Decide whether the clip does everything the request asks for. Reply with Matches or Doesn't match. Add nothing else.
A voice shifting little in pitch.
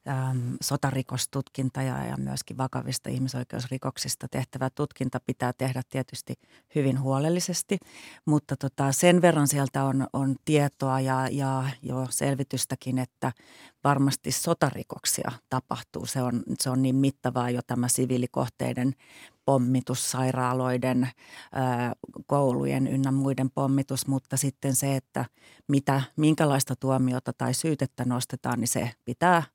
Matches